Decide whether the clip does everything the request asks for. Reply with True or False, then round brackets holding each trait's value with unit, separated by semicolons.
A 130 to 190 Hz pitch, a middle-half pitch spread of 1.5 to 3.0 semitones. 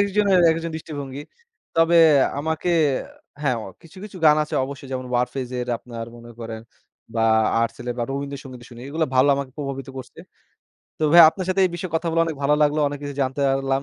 False (140 Hz; 3.9 semitones)